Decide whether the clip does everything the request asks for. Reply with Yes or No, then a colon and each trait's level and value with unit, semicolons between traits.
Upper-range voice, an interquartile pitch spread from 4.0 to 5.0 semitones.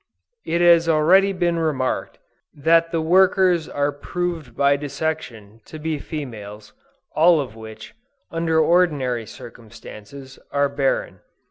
No: medium, 155 Hz; average, 4.4 semitones